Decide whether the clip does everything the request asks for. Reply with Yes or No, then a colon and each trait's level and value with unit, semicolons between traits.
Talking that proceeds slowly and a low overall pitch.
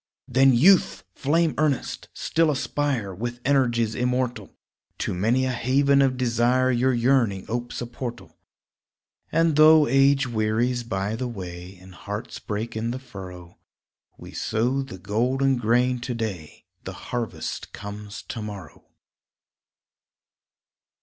Yes: slow, 130 wpm; low, 120 Hz